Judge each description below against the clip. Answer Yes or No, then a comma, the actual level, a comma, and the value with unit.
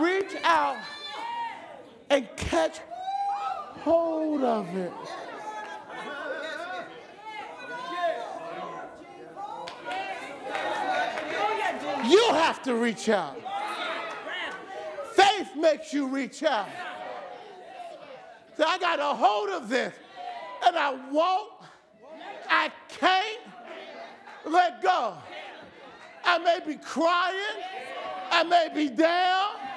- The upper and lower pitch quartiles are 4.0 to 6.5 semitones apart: Yes, average, 4.5 semitones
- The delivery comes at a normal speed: No, slow, 80 wpm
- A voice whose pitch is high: Yes, very high, 345 Hz